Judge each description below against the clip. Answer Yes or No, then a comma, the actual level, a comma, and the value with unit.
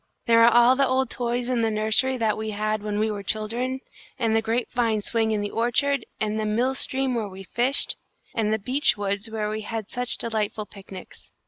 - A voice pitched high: Yes, high, 225 Hz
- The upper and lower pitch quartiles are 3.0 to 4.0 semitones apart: No, narrow, 2.5 semitones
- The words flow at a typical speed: No, fast, 215 wpm